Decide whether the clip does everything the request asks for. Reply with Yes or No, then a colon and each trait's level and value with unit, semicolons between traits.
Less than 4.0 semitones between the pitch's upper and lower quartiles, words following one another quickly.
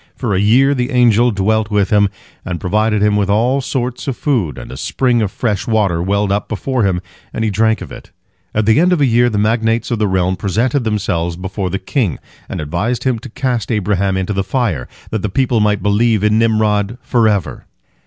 Yes: average, 3.3 semitones; fast, 215 wpm